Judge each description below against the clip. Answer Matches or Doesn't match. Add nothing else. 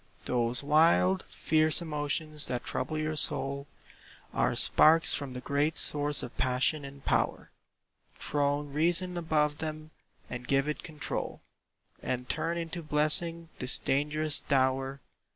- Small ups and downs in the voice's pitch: Matches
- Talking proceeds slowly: Matches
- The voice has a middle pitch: Matches